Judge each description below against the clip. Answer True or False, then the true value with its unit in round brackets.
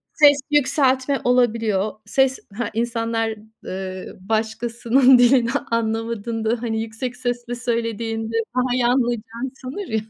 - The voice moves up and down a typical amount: False (2.1 semitones)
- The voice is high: True (235 Hz)